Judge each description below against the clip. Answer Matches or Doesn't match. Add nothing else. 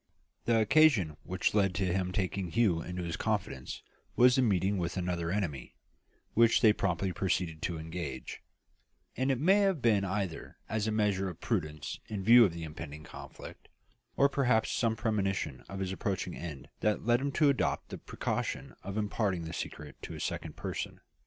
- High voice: Doesn't match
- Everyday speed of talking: Matches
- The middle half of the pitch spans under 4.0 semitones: Doesn't match